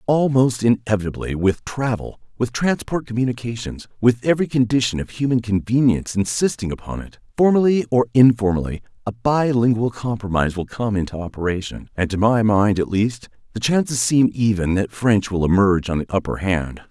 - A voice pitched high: No, low, 110 Hz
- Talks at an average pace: Yes, average, 160 wpm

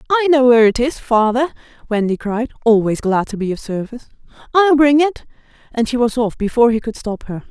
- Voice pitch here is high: Yes, high, 240 Hz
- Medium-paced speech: No, fast, 210 wpm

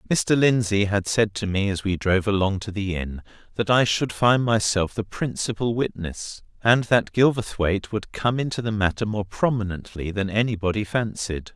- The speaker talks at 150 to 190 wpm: Yes, average, 175 wpm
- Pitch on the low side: Yes, low, 105 Hz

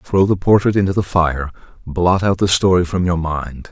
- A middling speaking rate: No, fast, 210 wpm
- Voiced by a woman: No, male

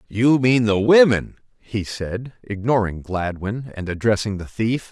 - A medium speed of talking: Yes, average, 145 wpm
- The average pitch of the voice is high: No, low, 110 Hz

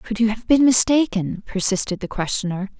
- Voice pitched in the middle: No, high, 210 Hz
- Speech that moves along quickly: No, average, 170 wpm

